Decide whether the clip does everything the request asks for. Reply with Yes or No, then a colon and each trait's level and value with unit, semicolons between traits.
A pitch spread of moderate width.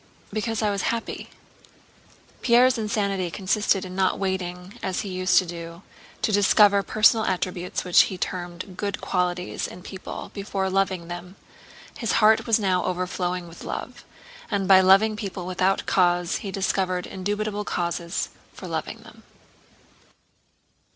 No: narrow, 2.2 semitones